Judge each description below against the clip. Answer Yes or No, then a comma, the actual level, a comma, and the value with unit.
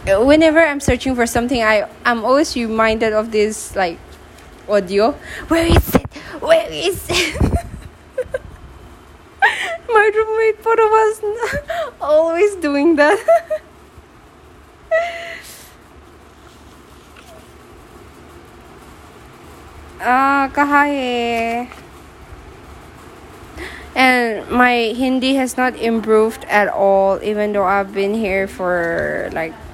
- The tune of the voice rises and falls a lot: Yes, wide, 7.0 semitones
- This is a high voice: Yes, very high, 260 Hz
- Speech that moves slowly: Yes, slow, 85 wpm